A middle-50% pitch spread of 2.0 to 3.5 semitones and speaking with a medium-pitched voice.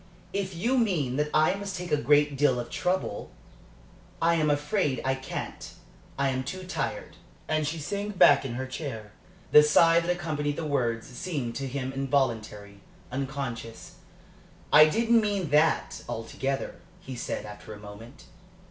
No: average, 4.7 semitones; medium, 145 Hz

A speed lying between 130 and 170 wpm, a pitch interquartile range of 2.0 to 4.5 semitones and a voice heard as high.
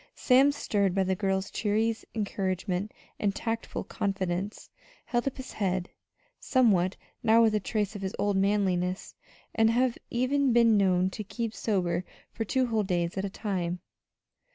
Yes: average, 155 wpm; average, 3.3 semitones; high, 205 Hz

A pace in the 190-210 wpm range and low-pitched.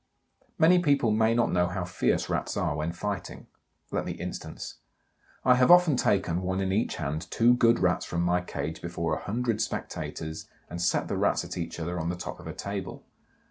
Yes: average, 200 wpm; very low, 95 Hz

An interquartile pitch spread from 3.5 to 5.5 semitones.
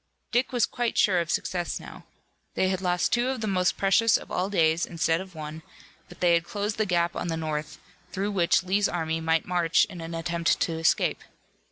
No: average, 3.1 semitones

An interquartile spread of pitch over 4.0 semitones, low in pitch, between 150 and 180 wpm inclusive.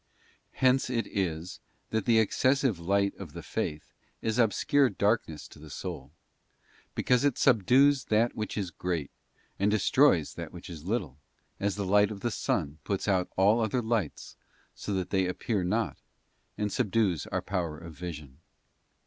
Yes: average, 4.7 semitones; low, 100 Hz; average, 165 wpm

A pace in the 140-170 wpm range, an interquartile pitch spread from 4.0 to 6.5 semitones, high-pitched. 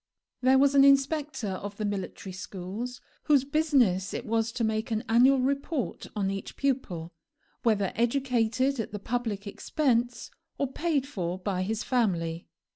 Yes: average, 150 wpm; average, 5.2 semitones; high, 230 Hz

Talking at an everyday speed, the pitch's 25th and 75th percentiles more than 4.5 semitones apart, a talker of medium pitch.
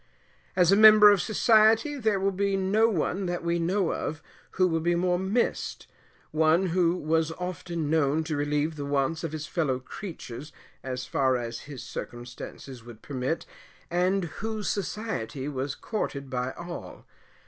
Yes: average, 160 wpm; average, 5.1 semitones; medium, 165 Hz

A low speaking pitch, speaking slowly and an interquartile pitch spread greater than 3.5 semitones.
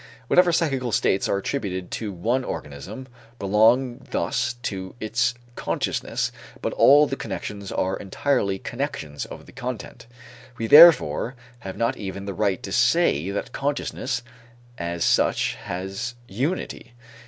Yes: low, 110 Hz; slow, 130 wpm; average, 5.2 semitones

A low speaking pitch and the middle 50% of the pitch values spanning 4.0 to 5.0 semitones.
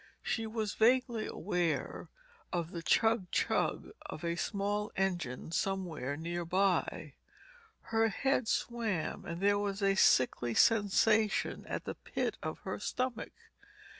No: high, 195 Hz; average, 4.4 semitones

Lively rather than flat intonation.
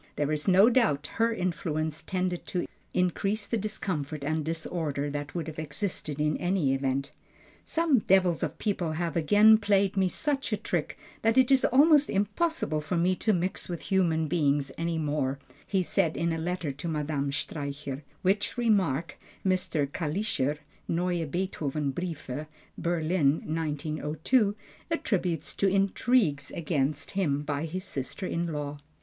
No: average, 4.6 semitones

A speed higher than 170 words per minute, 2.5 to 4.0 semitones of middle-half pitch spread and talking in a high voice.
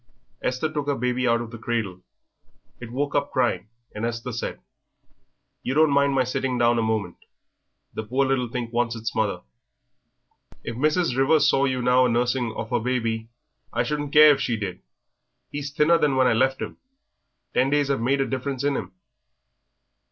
No: average, 185 wpm; average, 3.2 semitones; low, 125 Hz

